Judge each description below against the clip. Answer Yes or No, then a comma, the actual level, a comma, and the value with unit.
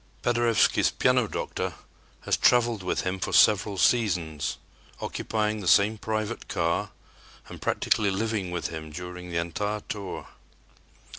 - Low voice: Yes, low, 100 Hz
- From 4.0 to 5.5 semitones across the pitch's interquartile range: No, average, 3.4 semitones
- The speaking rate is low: Yes, slow, 130 wpm